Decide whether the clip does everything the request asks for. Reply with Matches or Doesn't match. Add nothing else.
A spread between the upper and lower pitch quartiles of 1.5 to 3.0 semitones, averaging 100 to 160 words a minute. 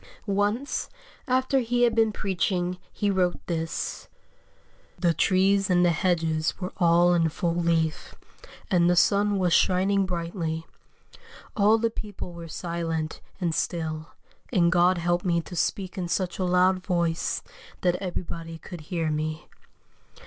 Matches